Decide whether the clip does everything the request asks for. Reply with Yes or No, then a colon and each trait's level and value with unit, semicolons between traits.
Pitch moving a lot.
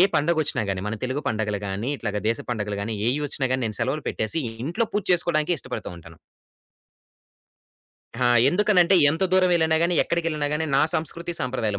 Yes: wide, 7.2 semitones